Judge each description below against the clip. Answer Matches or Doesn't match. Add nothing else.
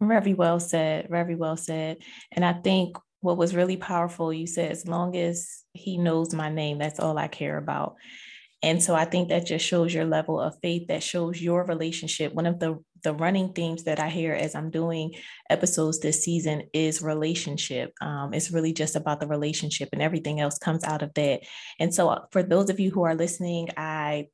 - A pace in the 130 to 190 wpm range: Doesn't match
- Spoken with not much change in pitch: Matches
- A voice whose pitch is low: Doesn't match